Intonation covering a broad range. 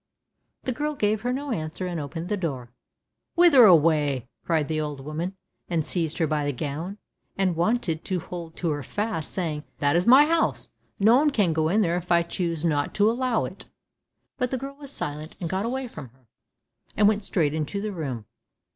Yes: wide, 5.9 semitones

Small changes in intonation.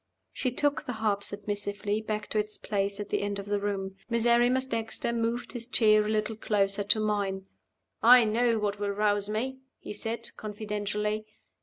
Yes: narrow, 2.0 semitones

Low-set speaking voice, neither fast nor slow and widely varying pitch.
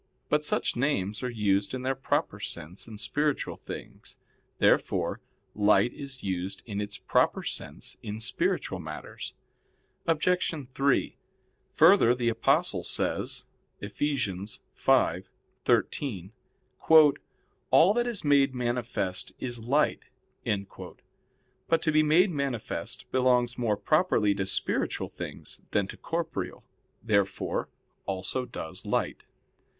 No: low, 120 Hz; slow, 115 wpm; wide, 6.2 semitones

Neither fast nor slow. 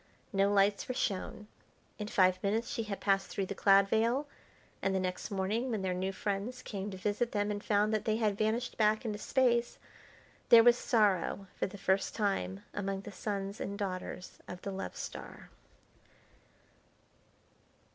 Yes: average, 170 wpm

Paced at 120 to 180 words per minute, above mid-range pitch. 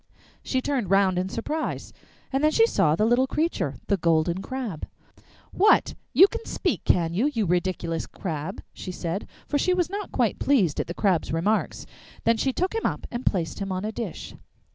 No: average, 190 wpm; high, 205 Hz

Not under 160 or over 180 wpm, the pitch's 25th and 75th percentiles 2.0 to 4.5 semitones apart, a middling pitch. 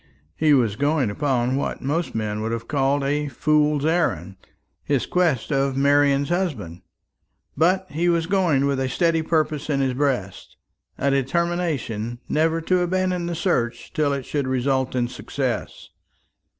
No: average, 150 wpm; average, 4.0 semitones; medium, 145 Hz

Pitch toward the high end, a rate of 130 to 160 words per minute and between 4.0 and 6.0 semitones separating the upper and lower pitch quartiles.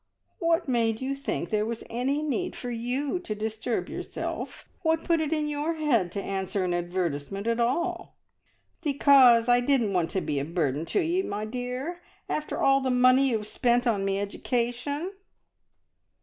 No: high, 245 Hz; average, 170 wpm; wide, 5.6 semitones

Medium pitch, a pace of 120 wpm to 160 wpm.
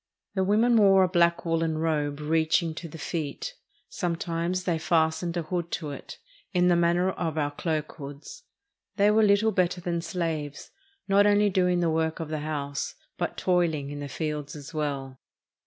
No: medium, 165 Hz; average, 180 wpm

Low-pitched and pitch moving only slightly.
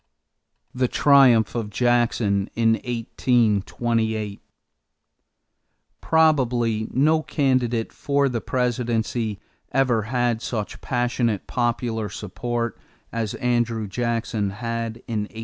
Yes: low, 115 Hz; narrow, 1.9 semitones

